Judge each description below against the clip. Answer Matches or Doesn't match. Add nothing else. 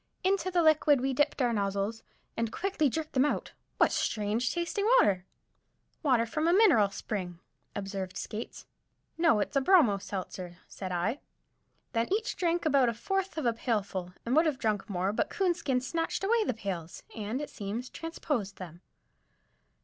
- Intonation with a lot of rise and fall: Matches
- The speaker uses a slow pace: Doesn't match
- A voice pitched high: Matches